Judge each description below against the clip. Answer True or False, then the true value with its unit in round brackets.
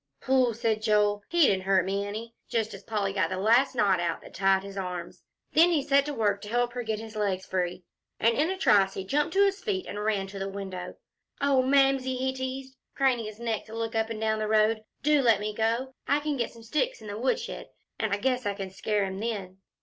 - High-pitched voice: True (220 Hz)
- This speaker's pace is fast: True (240 wpm)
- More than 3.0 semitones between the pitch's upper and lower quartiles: True (4.6 semitones)